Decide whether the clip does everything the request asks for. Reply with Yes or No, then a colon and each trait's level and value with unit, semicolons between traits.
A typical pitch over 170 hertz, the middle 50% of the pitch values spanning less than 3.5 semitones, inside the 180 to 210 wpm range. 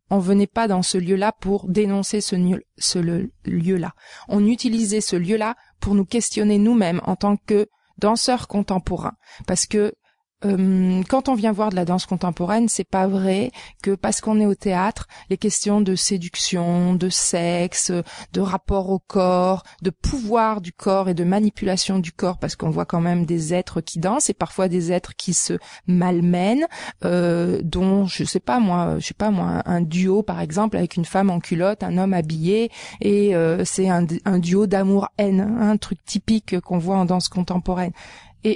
Yes: high, 190 Hz; narrow, 2.5 semitones; average, 185 wpm